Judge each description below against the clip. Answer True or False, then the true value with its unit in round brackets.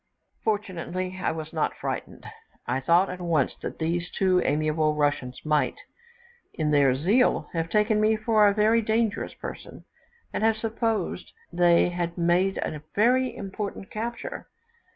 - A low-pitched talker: False (185 Hz)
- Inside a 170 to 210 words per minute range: False (145 wpm)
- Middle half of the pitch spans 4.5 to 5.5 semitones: True (5.1 semitones)